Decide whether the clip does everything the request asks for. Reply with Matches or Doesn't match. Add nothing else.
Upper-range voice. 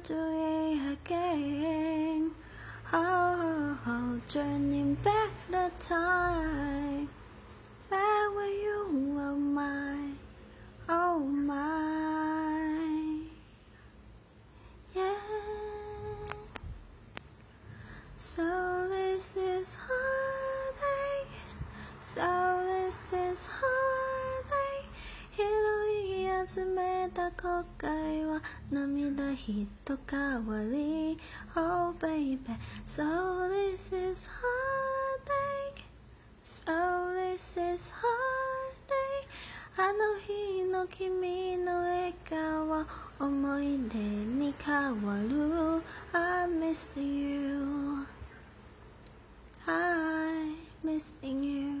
Matches